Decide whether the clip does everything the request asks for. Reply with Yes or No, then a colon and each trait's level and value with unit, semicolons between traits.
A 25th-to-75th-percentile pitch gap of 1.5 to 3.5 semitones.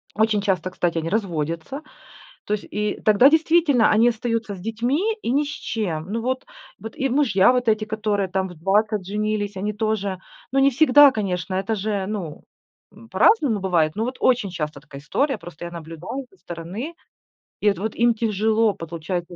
No: average, 4.7 semitones